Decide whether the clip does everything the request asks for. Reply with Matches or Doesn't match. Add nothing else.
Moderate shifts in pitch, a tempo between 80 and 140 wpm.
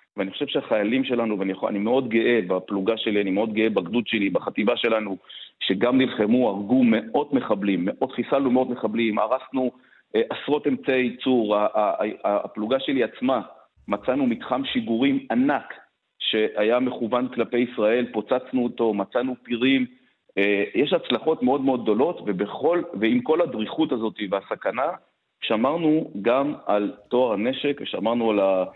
Doesn't match